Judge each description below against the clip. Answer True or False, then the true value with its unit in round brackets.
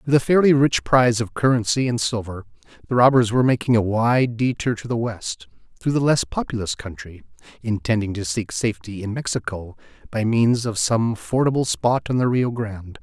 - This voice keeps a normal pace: True (185 wpm)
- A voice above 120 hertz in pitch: False (115 Hz)